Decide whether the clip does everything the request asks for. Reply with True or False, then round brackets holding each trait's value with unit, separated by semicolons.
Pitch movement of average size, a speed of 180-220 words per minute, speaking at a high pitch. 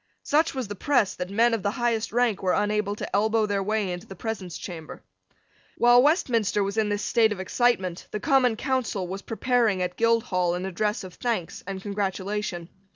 True (3.5 semitones; 190 wpm; 210 Hz)